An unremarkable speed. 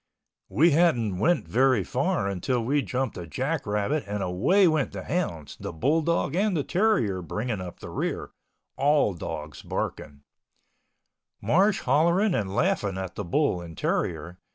Yes: average, 155 wpm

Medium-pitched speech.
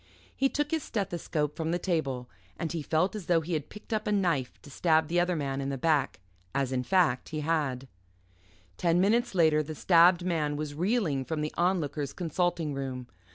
Yes: medium, 160 Hz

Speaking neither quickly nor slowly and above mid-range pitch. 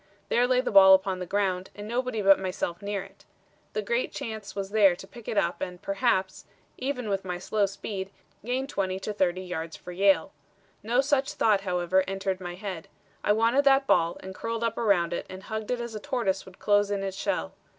No: fast, 215 wpm; high, 200 Hz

